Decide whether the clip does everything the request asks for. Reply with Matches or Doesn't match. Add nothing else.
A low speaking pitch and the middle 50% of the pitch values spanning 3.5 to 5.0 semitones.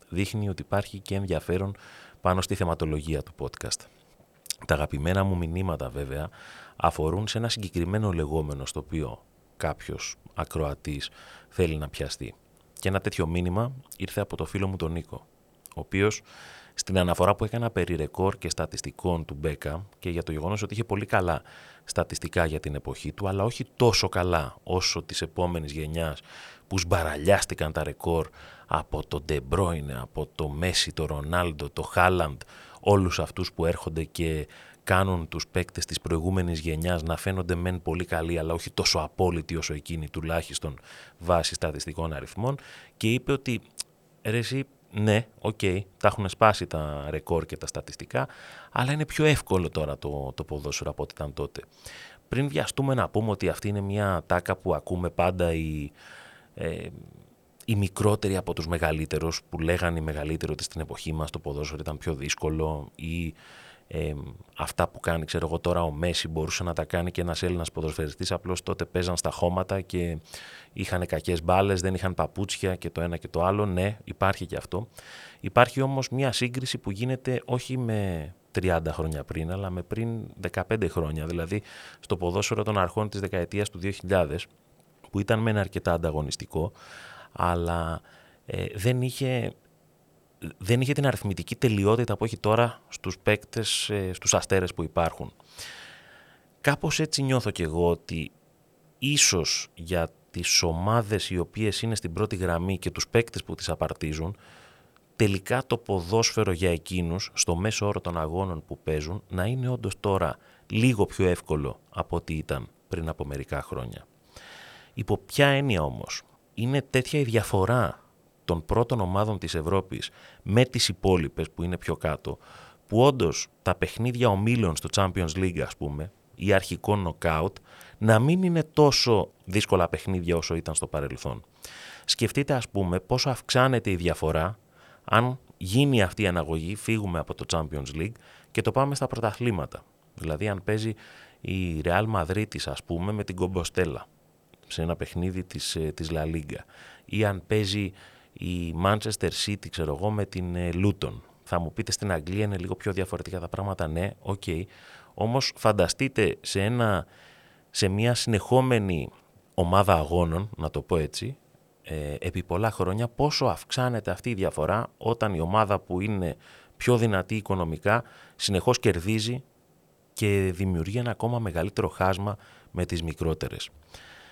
Matches